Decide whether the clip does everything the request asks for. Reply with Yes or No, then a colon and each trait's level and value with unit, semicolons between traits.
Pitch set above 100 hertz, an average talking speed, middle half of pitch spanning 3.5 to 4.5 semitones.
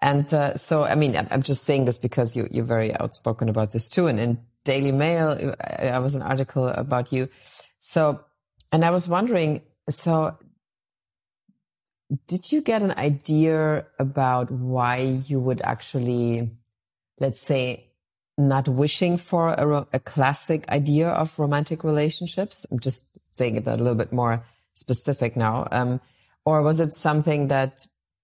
Yes: low, 135 Hz; average, 150 wpm; average, 3.8 semitones